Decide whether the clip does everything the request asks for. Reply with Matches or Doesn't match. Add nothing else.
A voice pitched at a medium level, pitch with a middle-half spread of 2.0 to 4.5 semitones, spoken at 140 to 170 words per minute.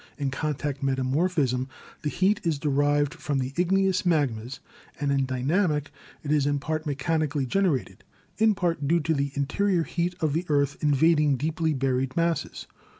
Matches